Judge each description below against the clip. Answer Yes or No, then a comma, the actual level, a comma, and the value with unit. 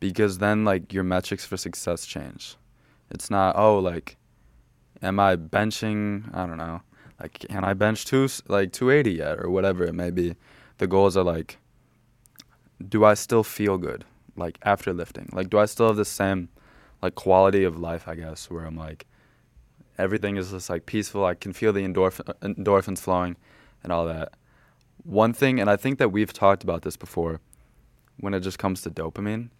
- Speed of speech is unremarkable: Yes, average, 185 wpm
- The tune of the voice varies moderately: Yes, average, 3.1 semitones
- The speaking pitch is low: Yes, very low, 95 Hz